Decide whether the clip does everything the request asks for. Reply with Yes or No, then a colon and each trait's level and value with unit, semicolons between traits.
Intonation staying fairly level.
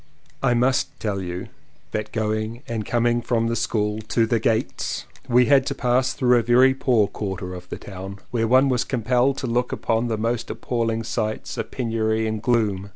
Yes: narrow, 2.3 semitones